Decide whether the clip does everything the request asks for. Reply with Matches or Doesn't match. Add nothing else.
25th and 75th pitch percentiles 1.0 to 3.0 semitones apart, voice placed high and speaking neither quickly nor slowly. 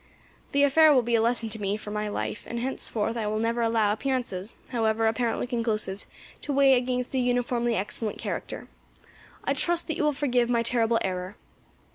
Matches